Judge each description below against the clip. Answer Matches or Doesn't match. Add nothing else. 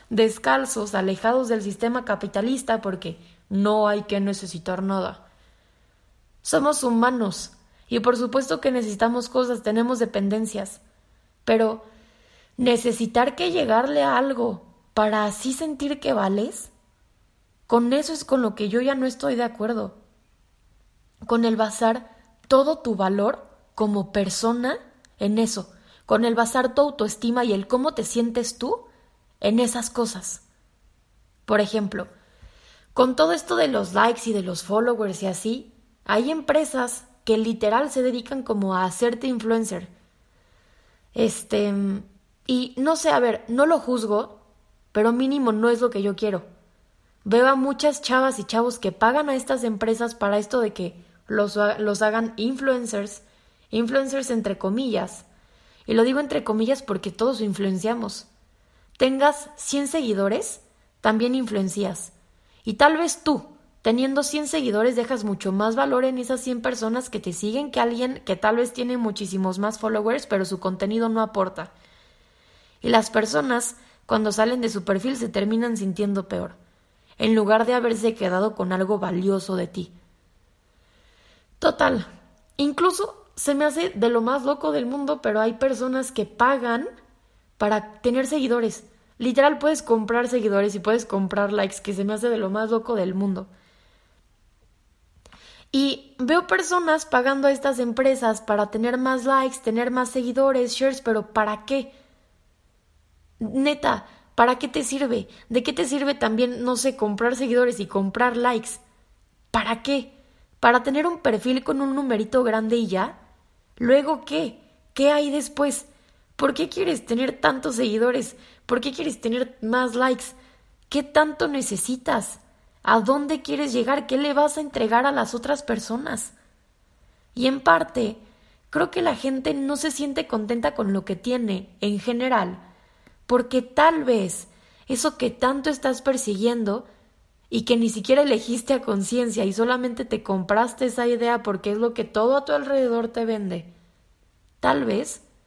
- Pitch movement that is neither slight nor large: Matches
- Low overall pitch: Doesn't match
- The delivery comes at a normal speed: Matches